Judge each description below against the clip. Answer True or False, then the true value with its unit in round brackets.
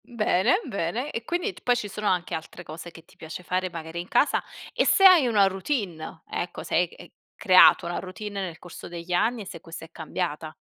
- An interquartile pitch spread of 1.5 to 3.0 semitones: False (4.4 semitones)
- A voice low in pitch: False (185 Hz)